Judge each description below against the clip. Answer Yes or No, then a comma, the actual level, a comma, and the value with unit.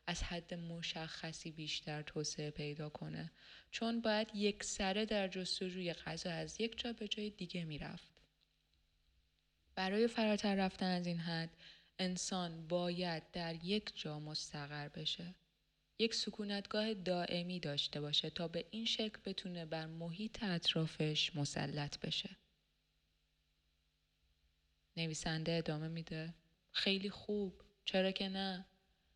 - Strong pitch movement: No, average, 4.1 semitones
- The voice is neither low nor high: Yes, medium, 170 Hz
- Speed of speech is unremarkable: Yes, average, 115 wpm